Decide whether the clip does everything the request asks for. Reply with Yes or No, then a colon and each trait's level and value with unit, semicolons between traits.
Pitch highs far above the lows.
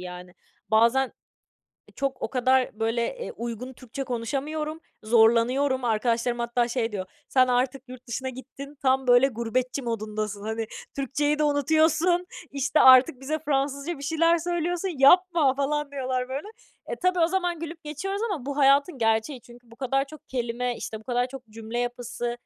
No: average, 3.8 semitones